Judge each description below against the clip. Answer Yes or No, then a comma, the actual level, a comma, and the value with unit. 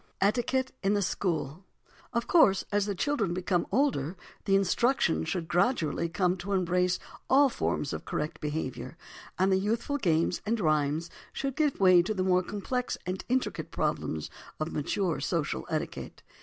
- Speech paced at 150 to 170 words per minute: Yes, average, 155 wpm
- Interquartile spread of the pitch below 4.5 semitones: No, average, 5.3 semitones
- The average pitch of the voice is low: No, high, 190 Hz